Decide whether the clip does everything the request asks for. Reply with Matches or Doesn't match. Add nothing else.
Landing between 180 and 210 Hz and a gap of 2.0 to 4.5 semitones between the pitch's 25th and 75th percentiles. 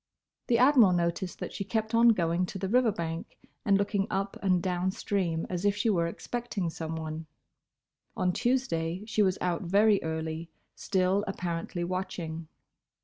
Matches